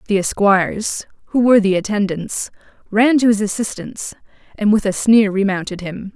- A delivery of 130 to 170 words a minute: Yes, average, 155 wpm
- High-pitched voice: Yes, high, 205 Hz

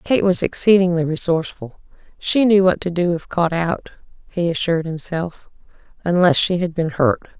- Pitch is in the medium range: Yes, medium, 175 Hz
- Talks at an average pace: Yes, average, 155 wpm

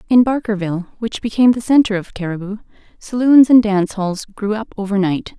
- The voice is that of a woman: Yes, female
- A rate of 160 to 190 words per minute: Yes, average, 165 wpm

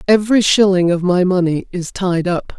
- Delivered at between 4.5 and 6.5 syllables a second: Yes, 5.0 syllables/s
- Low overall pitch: No, medium, 185 Hz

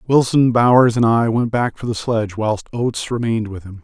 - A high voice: No, low, 115 Hz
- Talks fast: Yes, fast, 220 wpm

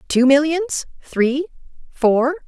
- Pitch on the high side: Yes, very high, 285 Hz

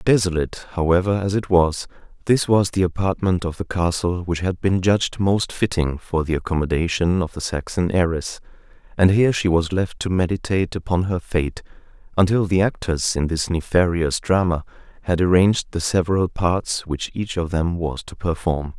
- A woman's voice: No, male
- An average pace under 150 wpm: No, average, 170 wpm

